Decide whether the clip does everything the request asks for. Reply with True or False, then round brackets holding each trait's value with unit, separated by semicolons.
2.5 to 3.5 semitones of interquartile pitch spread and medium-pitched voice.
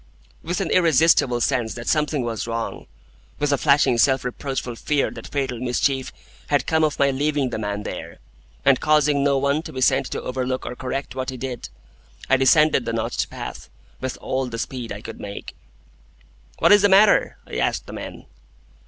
False (3.2 semitones; 130 Hz)